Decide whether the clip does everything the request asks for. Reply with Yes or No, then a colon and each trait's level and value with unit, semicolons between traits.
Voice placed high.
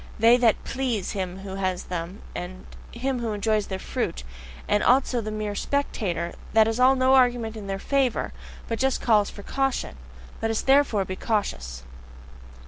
Yes: high, 220 Hz